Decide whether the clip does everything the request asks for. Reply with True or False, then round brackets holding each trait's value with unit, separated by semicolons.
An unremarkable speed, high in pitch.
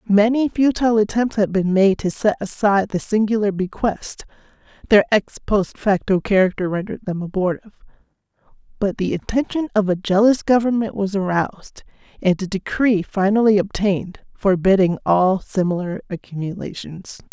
False (130 wpm; 200 Hz)